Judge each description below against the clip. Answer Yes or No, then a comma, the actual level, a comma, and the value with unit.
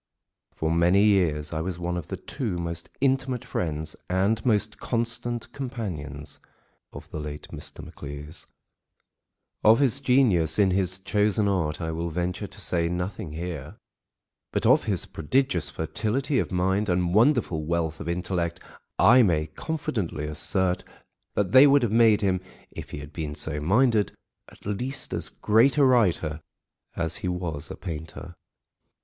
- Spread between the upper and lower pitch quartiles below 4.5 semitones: No, average, 5.3 semitones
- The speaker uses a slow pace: No, average, 155 wpm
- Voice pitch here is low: Yes, very low, 90 Hz